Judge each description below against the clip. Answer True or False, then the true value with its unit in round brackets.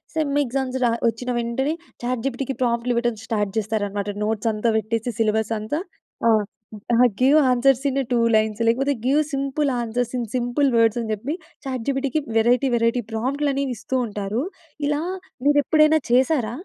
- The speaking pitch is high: True (245 Hz)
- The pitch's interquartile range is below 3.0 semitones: False (3.3 semitones)